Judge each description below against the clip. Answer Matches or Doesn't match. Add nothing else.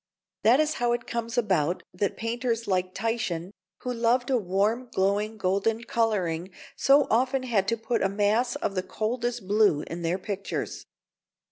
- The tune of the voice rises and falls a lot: Doesn't match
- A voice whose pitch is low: Doesn't match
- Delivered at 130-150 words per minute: Doesn't match